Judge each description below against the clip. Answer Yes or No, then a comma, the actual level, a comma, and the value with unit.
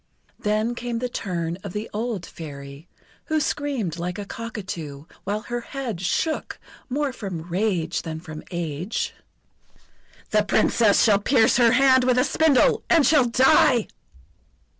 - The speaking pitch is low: No, high, 215 Hz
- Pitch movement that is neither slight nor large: No, wide, 6.3 semitones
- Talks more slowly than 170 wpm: Yes, average, 140 wpm